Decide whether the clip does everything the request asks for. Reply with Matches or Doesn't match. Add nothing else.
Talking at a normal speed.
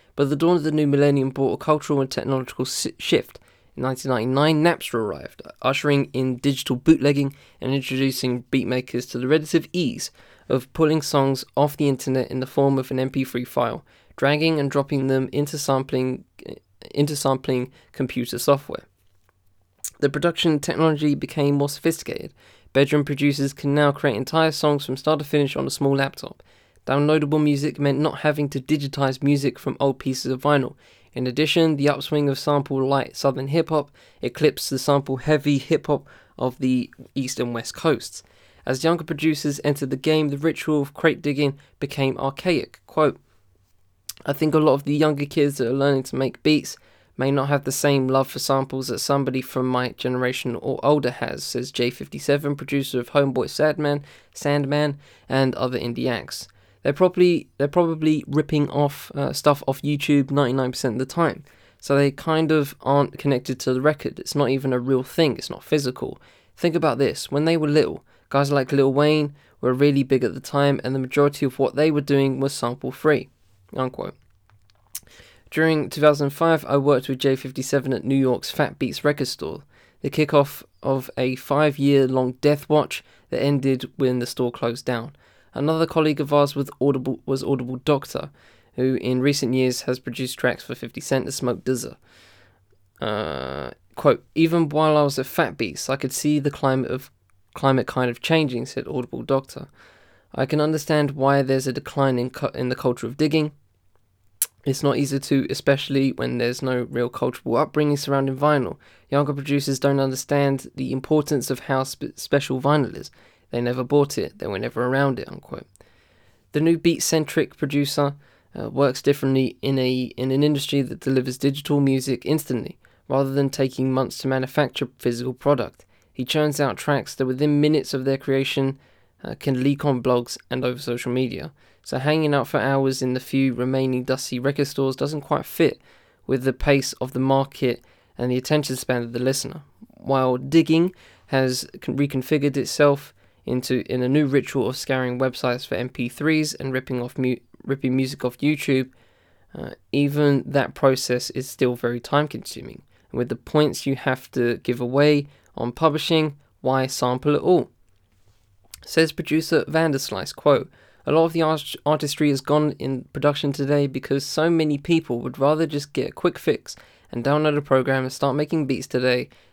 Matches